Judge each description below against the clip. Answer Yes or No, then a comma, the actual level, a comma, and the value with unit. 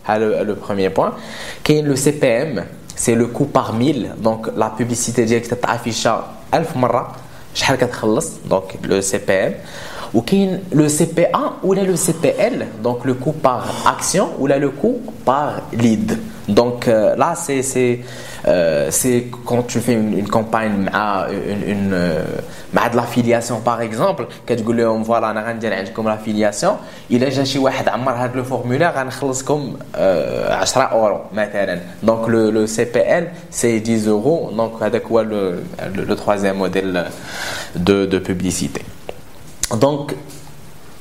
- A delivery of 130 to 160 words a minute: Yes, average, 145 wpm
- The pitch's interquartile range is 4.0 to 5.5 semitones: No, average, 3.4 semitones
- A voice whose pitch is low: Yes, low, 120 Hz